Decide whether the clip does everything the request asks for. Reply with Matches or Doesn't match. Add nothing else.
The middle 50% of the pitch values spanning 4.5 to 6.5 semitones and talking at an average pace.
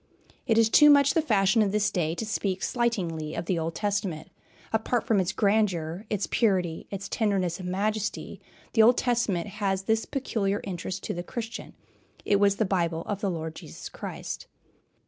Doesn't match